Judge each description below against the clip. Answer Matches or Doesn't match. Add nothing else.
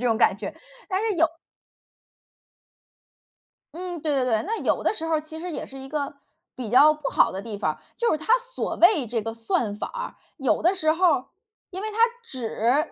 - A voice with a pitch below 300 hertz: Doesn't match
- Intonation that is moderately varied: Doesn't match